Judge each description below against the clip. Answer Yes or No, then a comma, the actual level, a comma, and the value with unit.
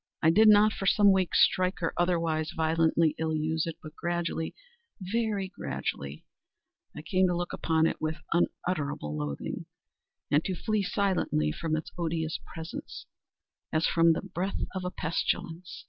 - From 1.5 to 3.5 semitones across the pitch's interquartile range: Yes, average, 2.9 semitones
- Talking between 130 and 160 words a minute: Yes, average, 145 wpm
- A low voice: No, medium, 170 Hz